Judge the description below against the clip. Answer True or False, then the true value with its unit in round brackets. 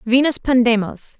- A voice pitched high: True (240 Hz)